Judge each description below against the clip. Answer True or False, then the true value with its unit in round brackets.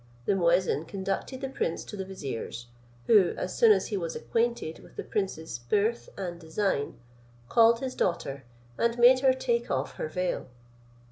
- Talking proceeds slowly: False (165 wpm)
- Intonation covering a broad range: True (6.3 semitones)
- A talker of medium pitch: False (195 Hz)